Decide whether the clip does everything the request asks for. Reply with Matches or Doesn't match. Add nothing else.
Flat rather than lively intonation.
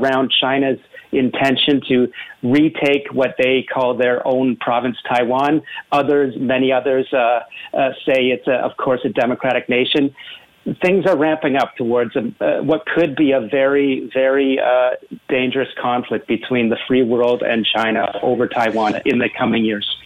Matches